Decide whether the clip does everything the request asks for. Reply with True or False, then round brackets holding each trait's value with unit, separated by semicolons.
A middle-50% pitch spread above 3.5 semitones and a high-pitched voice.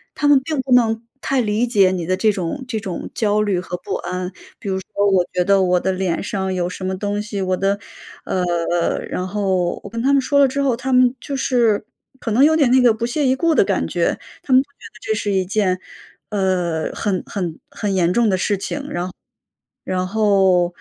True (4.8 semitones; 200 Hz)